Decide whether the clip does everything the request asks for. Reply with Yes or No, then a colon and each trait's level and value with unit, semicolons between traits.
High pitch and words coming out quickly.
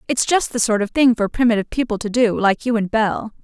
Yes: high, 225 Hz; fast, 260 wpm